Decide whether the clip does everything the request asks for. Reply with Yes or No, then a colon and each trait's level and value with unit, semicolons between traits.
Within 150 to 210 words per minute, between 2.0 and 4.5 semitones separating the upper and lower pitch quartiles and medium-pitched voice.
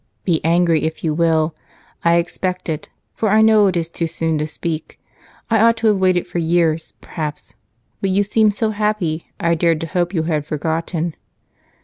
Yes: average, 185 wpm; average, 3.3 semitones; medium, 170 Hz